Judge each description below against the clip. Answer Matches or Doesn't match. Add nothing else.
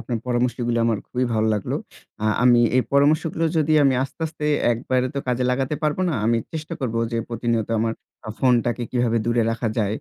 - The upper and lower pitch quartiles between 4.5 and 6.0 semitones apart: Doesn't match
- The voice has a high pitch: Doesn't match